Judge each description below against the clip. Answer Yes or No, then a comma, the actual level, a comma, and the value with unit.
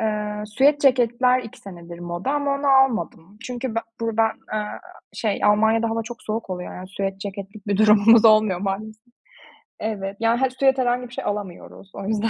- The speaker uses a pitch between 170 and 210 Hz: No, high, 220 Hz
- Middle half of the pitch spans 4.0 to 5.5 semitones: No, average, 3.3 semitones